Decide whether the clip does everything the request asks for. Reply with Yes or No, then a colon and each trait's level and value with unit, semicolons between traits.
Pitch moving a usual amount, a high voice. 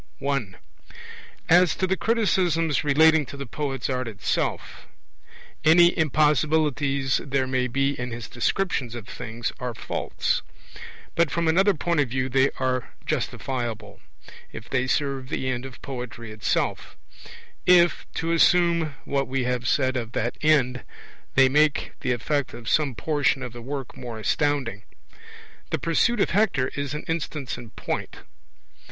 No: average, 4.0 semitones; low, 135 Hz